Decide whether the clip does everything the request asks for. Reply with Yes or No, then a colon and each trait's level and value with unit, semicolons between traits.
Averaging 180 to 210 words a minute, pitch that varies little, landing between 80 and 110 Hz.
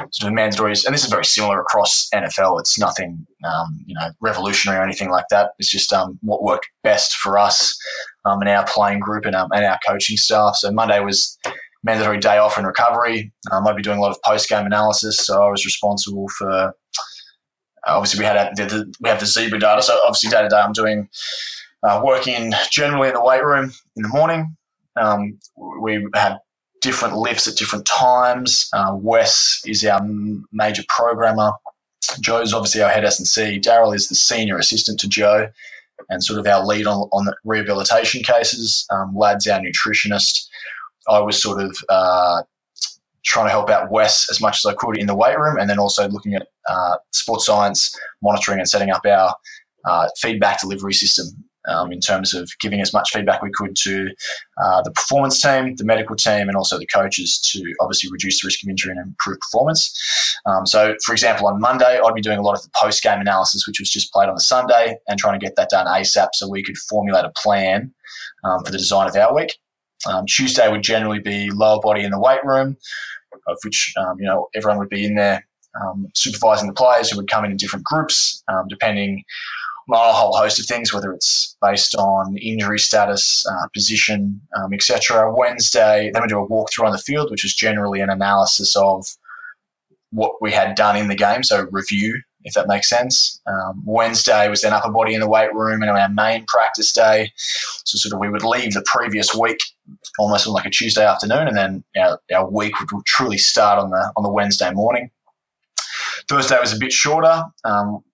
Yes: fast, 205 wpm; narrow, 2.0 semitones; low, 105 Hz